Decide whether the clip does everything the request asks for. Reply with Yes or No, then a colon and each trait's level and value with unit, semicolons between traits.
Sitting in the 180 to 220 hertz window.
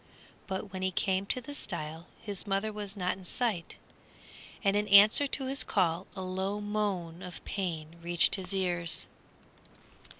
Yes: high, 190 Hz